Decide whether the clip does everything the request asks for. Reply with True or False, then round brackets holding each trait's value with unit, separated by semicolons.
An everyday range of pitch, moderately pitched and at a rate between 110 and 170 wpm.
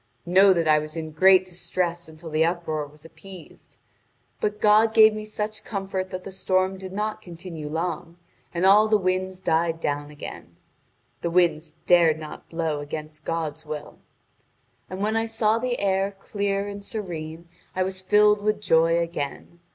True (3.8 semitones; 180 Hz; 165 wpm)